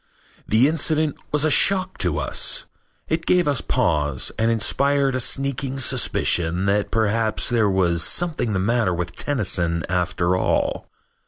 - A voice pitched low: Yes, low, 115 Hz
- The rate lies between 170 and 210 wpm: No, average, 145 wpm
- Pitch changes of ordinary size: No, wide, 7.8 semitones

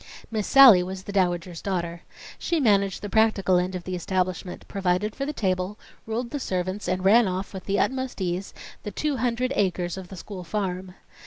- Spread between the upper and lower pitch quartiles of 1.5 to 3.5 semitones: Yes, average, 3.1 semitones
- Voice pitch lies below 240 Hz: Yes, high, 190 Hz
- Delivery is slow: No, average, 190 wpm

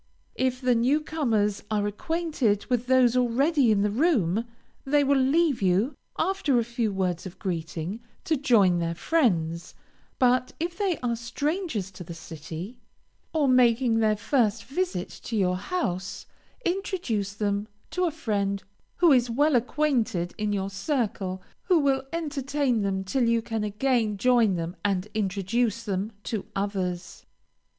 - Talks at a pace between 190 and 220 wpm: No, average, 150 wpm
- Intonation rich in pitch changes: Yes, wide, 5.7 semitones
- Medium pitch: No, high, 230 Hz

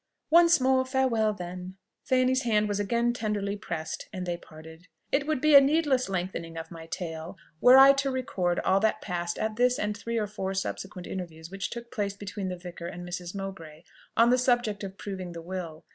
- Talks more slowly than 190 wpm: No, average, 200 wpm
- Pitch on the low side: No, high, 200 Hz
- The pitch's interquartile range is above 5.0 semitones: Yes, wide, 5.5 semitones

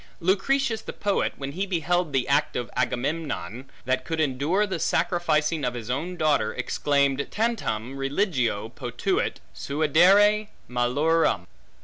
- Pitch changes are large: Yes, wide, 5.8 semitones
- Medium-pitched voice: Yes, medium, 150 Hz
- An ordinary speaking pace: No, slow, 125 wpm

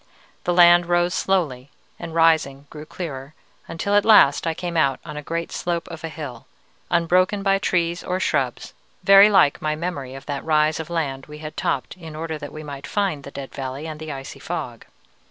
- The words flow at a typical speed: Yes, average, 195 wpm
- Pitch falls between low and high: Yes, medium, 160 Hz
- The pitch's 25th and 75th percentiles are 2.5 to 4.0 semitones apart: Yes, average, 3.4 semitones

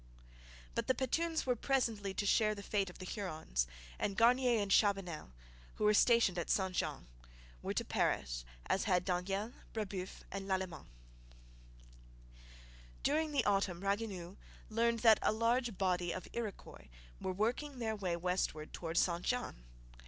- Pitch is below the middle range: No, high, 200 Hz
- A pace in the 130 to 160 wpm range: Yes, average, 150 wpm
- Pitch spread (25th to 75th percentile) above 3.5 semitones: Yes, average, 4.1 semitones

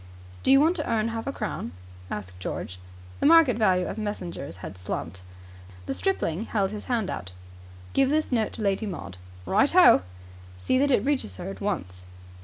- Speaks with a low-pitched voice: No, high, 210 Hz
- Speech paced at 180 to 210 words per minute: Yes, average, 185 wpm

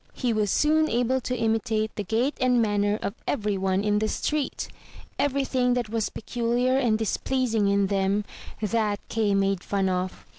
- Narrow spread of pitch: No, average, 3.5 semitones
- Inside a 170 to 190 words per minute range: Yes, average, 180 wpm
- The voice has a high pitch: Yes, high, 220 Hz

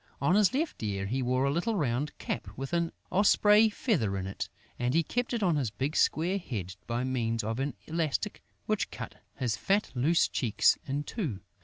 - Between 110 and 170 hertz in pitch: Yes, medium, 140 Hz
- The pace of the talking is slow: No, average, 195 wpm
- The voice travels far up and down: Yes, wide, 7.3 semitones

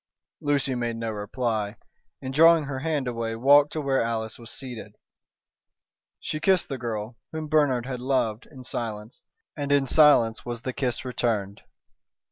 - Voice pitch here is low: Yes, low, 125 Hz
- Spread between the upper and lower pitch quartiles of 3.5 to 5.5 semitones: Yes, average, 3.8 semitones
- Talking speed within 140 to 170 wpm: Yes, average, 155 wpm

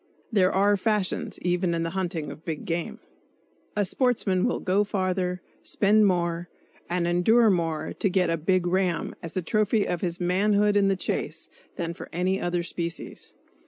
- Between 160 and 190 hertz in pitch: Yes, medium, 185 Hz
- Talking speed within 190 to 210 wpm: No, average, 170 wpm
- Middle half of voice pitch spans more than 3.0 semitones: No, average, 2.7 semitones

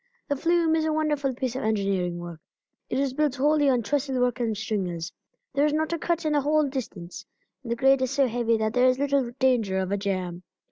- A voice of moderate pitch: No, very high, 255 Hz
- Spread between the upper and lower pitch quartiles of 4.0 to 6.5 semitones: Yes, average, 5.2 semitones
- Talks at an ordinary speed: No, fast, 230 wpm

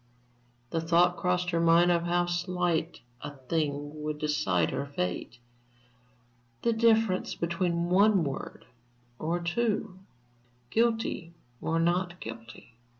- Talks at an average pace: No, slow, 115 wpm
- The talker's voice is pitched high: No, medium, 170 Hz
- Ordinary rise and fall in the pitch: Yes, average, 3.0 semitones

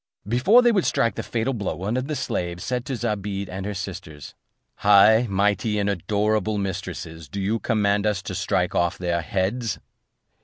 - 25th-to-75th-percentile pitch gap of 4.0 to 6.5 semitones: No, average, 3.2 semitones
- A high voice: No, low, 100 Hz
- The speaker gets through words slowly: No, average, 180 wpm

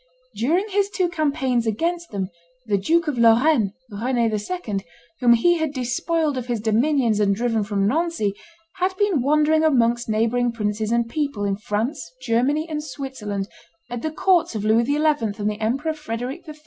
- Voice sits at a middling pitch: No, high, 245 Hz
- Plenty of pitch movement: Yes, wide, 6.0 semitones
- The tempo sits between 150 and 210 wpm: Yes, average, 170 wpm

